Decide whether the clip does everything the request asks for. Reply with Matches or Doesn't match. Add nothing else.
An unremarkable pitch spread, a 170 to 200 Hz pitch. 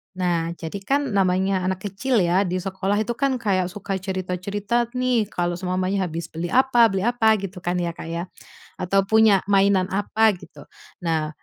Matches